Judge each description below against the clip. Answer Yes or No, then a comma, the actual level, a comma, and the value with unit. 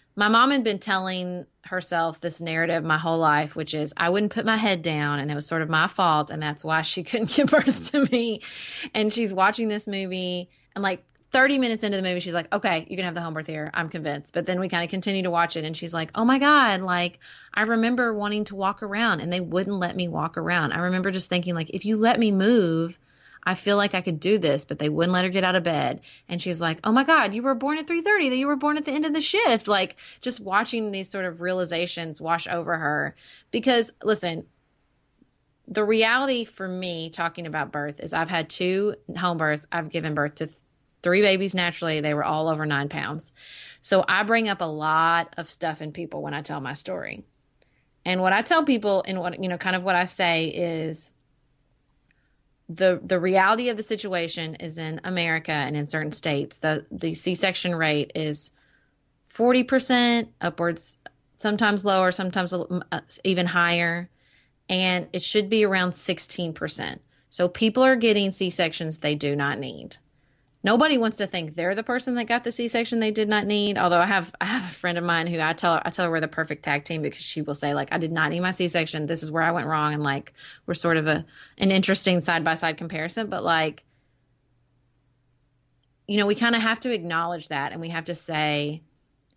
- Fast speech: Yes, fast, 220 wpm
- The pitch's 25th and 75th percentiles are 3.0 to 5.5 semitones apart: Yes, average, 4.3 semitones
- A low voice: No, medium, 175 Hz